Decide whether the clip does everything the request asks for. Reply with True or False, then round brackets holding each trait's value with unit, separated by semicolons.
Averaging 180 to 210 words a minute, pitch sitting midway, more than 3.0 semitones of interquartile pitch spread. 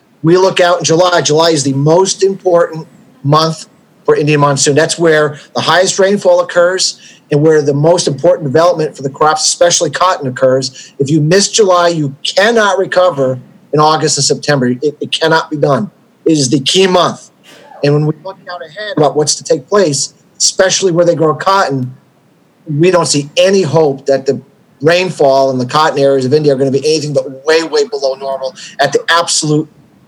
True (190 wpm; 160 Hz; 3.7 semitones)